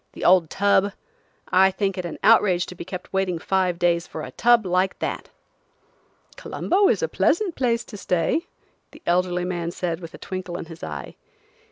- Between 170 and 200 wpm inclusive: Yes, average, 185 wpm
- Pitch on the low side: No, medium, 185 Hz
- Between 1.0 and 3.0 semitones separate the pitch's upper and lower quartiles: Yes, narrow, 2.6 semitones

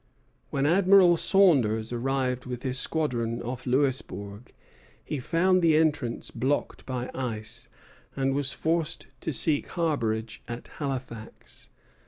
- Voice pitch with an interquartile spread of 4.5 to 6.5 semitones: Yes, average, 4.9 semitones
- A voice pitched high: No, low, 135 Hz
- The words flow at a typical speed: No, slow, 120 wpm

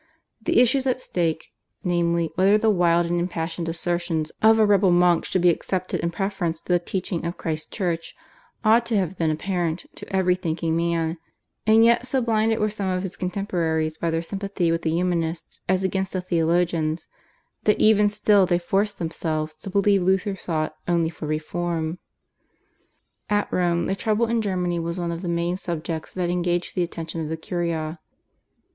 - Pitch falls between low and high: Yes, medium, 175 Hz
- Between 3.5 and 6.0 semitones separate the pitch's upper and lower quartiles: No, average, 2.8 semitones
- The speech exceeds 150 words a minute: Yes, average, 180 wpm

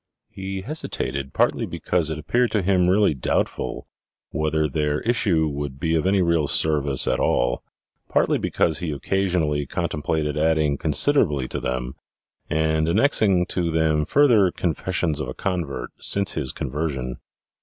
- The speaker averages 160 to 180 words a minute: No, average, 145 wpm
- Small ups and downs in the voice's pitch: No, average, 4.1 semitones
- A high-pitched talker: No, very low, 80 Hz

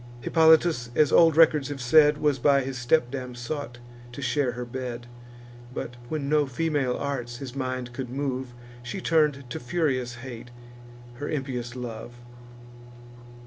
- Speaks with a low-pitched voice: Yes, low, 130 Hz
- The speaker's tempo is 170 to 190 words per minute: No, average, 145 wpm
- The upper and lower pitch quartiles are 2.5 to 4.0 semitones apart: Yes, average, 3.2 semitones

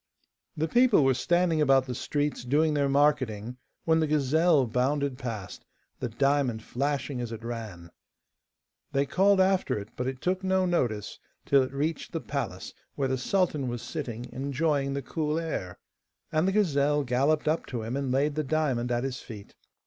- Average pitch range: Yes, average, 4.0 semitones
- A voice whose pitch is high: No, medium, 140 Hz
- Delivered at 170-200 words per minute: Yes, average, 175 wpm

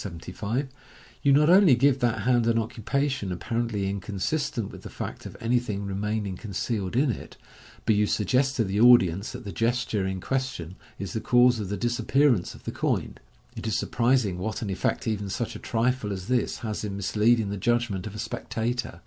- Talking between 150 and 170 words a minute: No, average, 200 wpm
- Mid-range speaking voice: No, low, 110 Hz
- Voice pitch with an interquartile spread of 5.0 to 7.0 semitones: No, average, 3.6 semitones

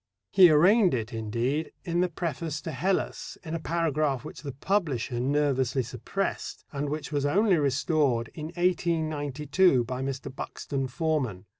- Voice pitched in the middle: Yes, medium, 150 Hz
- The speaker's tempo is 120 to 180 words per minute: Yes, average, 145 wpm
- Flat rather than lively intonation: No, average, 4.2 semitones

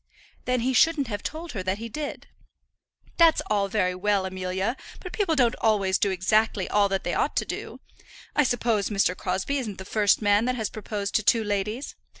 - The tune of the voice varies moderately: Yes, average, 4.1 semitones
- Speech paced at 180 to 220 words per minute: Yes, average, 195 wpm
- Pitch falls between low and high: No, high, 210 Hz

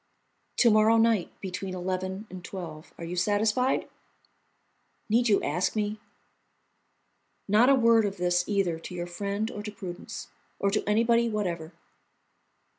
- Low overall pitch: No, high, 200 Hz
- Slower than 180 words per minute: Yes, average, 140 wpm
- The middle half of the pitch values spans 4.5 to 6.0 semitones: No, average, 3.5 semitones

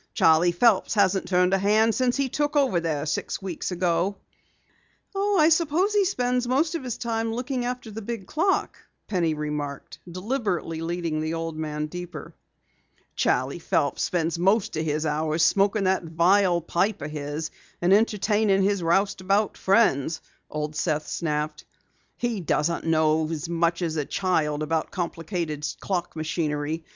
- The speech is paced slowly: No, average, 150 wpm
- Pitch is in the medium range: Yes, medium, 175 Hz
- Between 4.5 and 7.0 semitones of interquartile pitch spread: Yes, wide, 5.4 semitones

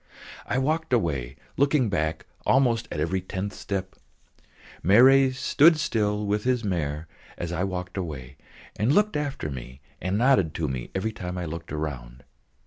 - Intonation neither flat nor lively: No, wide, 8.2 semitones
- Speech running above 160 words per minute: No, average, 155 wpm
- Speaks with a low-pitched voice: Yes, very low, 95 Hz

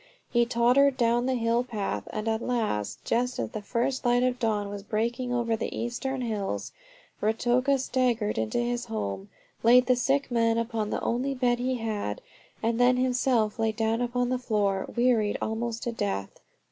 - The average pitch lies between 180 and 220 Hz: No, high, 235 Hz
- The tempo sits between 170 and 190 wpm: Yes, average, 175 wpm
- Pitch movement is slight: Yes, narrow, 2.2 semitones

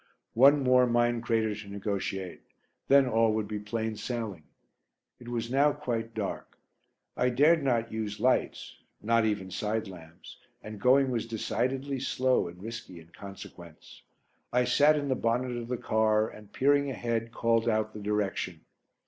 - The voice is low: Yes, low, 115 Hz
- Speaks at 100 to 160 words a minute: Yes, average, 155 wpm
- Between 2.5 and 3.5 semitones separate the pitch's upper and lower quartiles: Yes, average, 3.2 semitones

